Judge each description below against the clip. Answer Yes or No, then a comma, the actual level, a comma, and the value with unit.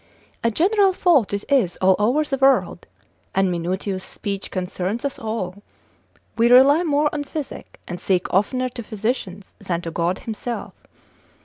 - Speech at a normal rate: Yes, average, 150 wpm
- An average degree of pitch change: No, wide, 6.3 semitones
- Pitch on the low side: No, high, 220 Hz